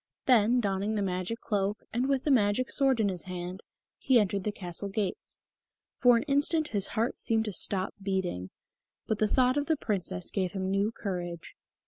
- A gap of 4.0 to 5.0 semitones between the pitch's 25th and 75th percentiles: Yes, average, 4.3 semitones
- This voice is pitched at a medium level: No, high, 205 Hz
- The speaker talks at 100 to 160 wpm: No, average, 185 wpm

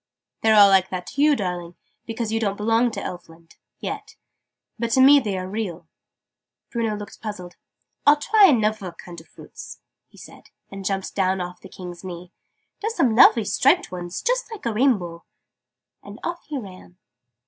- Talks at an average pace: Yes, average, 175 wpm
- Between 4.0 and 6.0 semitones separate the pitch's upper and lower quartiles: Yes, average, 4.6 semitones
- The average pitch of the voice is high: Yes, high, 205 Hz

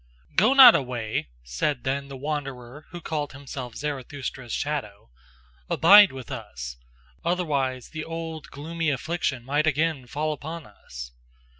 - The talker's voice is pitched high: No, medium, 140 Hz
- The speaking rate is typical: No, slow, 130 wpm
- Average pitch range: Yes, average, 4.1 semitones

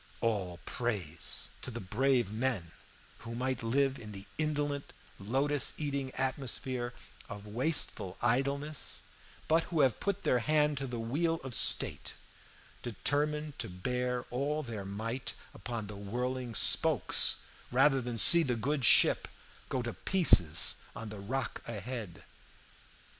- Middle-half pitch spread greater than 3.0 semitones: Yes, average, 4.2 semitones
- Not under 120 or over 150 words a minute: Yes, slow, 135 wpm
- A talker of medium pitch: No, low, 125 Hz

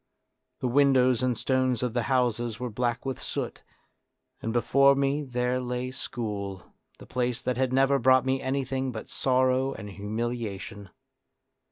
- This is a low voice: Yes, low, 125 Hz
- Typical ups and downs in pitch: No, narrow, 1.8 semitones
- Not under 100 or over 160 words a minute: No, average, 175 wpm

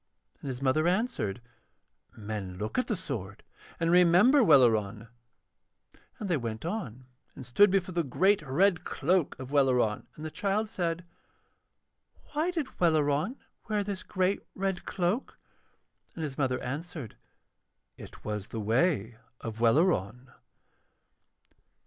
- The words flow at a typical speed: No, slow, 130 wpm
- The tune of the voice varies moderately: No, wide, 7.7 semitones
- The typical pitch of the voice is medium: Yes, medium, 155 Hz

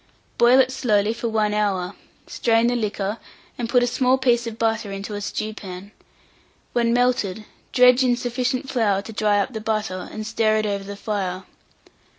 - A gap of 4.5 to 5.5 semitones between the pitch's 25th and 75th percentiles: No, average, 3.0 semitones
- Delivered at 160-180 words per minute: Yes, average, 175 wpm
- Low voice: No, high, 220 Hz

